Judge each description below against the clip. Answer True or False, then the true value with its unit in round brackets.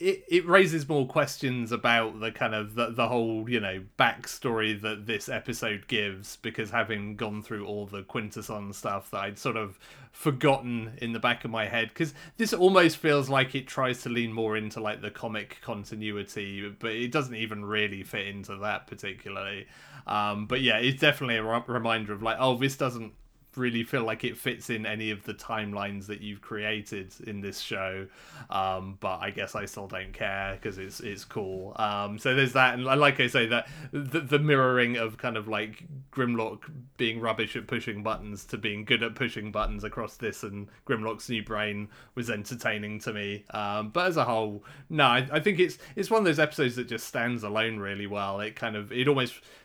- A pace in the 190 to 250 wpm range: True (200 wpm)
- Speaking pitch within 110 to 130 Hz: True (115 Hz)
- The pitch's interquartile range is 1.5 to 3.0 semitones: False (3.6 semitones)